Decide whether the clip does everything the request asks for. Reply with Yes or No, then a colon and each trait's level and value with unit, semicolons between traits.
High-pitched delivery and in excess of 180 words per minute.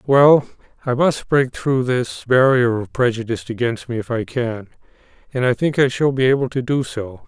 No: low, 125 Hz; average, 200 wpm